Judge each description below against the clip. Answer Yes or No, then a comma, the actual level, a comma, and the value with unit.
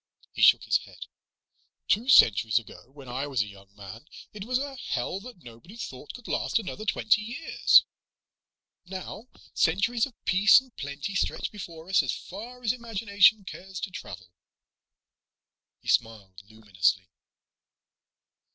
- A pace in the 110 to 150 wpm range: Yes, average, 145 wpm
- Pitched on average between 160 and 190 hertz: Yes, medium, 185 Hz